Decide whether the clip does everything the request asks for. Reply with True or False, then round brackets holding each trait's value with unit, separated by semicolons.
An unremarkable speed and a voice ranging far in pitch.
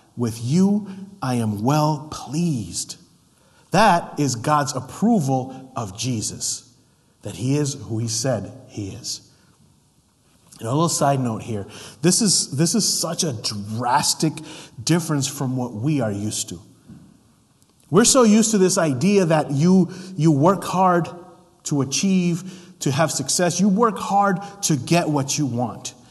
True (145 wpm; 6.2 semitones)